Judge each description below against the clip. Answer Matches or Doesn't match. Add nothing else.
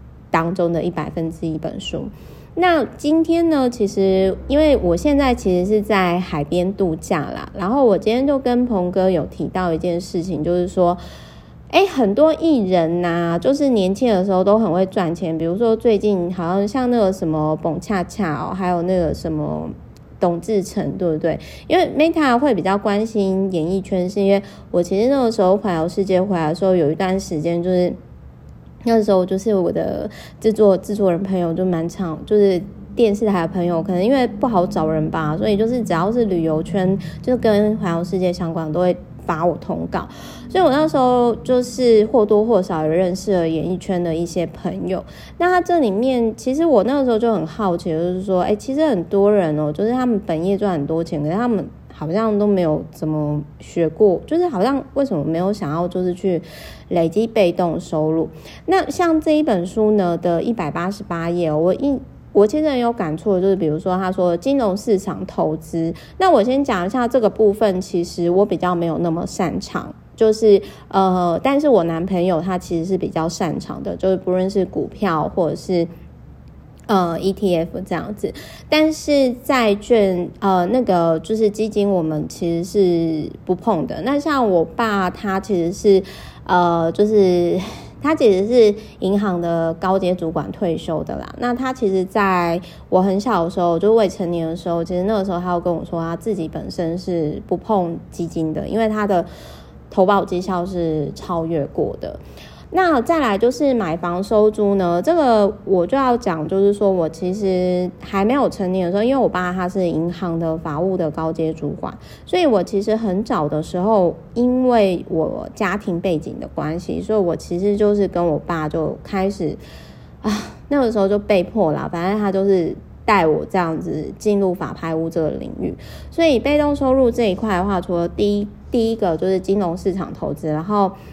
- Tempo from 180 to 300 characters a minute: Matches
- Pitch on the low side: Doesn't match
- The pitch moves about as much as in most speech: Matches